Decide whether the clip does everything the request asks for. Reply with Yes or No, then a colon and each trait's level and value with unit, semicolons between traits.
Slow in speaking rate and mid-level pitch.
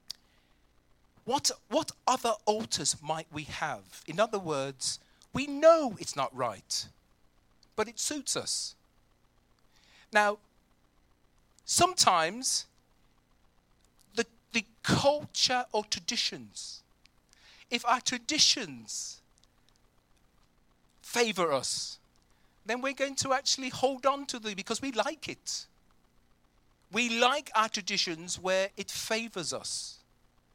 Yes: slow, 100 wpm; medium, 160 Hz